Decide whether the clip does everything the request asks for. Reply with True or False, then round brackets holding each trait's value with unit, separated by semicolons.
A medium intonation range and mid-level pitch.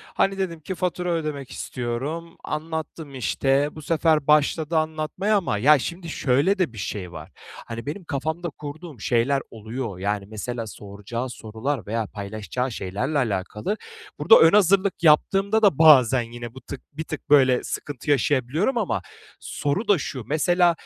False (5.7 semitones; 145 Hz)